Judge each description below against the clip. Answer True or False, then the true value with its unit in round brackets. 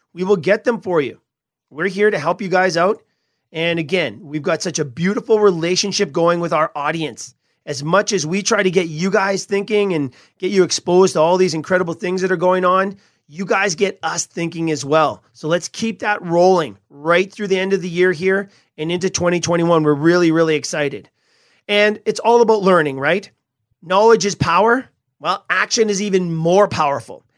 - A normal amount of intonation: True (3.6 semitones)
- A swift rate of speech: False (195 wpm)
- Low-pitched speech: False (180 Hz)